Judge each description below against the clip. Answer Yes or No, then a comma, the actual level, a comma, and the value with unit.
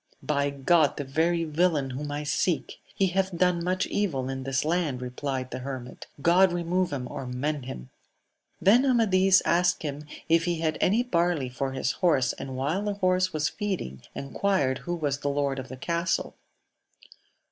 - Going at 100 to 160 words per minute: No, average, 180 wpm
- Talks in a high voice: No, medium, 155 Hz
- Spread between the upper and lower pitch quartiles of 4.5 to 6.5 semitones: Yes, average, 5.0 semitones